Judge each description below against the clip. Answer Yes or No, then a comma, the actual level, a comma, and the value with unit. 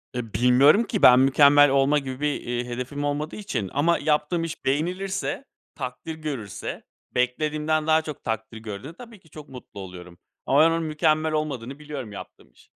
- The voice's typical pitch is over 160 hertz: No, medium, 145 Hz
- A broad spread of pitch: No, average, 3.9 semitones